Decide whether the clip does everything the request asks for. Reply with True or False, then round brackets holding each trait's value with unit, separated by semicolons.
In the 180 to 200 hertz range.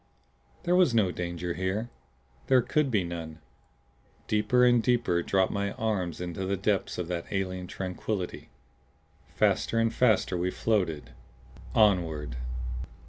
False (95 Hz)